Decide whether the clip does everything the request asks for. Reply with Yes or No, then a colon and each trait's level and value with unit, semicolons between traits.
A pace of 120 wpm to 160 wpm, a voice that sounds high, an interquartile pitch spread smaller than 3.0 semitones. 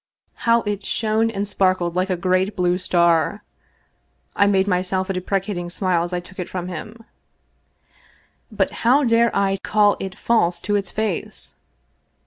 Yes: average, 155 wpm; high, 195 Hz; narrow, 2.4 semitones